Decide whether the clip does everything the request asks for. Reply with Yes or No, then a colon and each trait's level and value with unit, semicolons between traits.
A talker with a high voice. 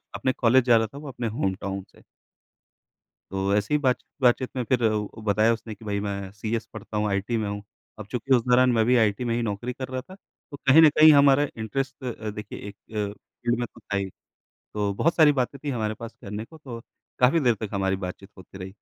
No: low, 115 Hz